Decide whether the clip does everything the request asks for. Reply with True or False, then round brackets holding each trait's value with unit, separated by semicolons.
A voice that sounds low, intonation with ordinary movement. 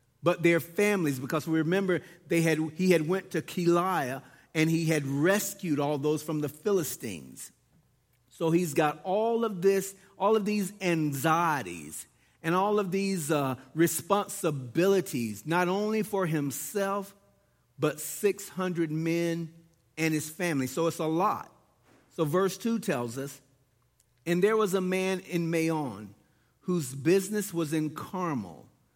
False (165 Hz; 4.3 semitones)